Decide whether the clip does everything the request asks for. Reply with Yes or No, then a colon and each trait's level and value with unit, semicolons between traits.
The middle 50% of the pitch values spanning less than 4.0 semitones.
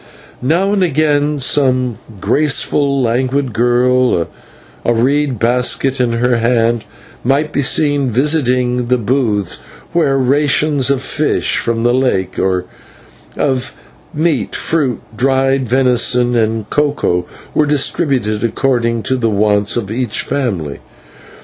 Yes: average, 3.3 semitones